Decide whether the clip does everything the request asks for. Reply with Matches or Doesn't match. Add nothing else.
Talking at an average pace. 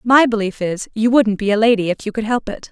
Doesn't match